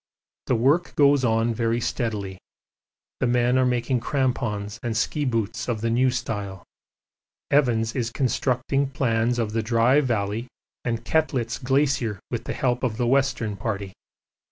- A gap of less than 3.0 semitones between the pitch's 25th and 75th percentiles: Yes, narrow, 2.6 semitones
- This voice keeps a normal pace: Yes, average, 150 wpm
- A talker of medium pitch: No, low, 120 Hz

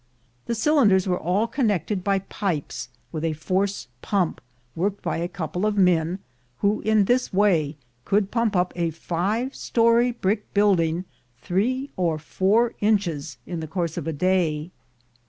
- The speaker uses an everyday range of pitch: Yes, average, 3.9 semitones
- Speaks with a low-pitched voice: No, high, 190 Hz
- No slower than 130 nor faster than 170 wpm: Yes, average, 155 wpm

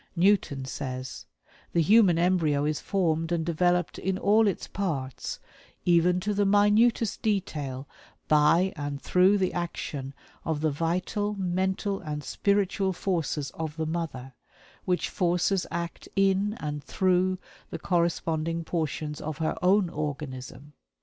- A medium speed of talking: No, slow, 130 wpm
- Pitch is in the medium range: Yes, medium, 170 Hz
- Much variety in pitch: No, average, 4.1 semitones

